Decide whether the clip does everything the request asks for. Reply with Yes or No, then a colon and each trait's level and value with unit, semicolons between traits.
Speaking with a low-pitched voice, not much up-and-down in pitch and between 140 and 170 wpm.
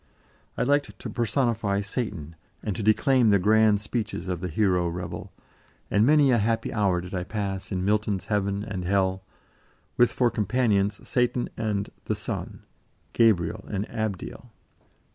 No: low, 105 Hz; average, 3.1 semitones; average, 150 wpm